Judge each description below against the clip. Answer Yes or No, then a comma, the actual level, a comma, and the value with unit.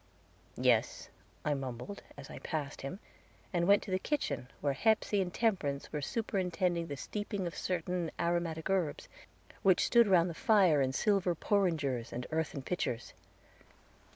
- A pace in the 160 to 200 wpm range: No, average, 150 wpm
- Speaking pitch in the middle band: Yes, medium, 175 Hz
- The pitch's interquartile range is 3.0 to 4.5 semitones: No, average, 5.0 semitones